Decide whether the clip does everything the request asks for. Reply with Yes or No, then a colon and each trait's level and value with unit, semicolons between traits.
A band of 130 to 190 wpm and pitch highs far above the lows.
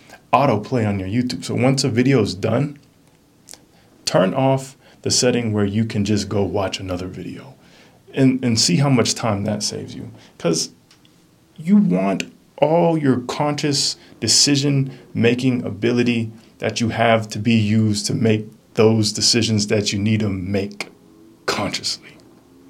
No: average, 150 wpm; average, 4.1 semitones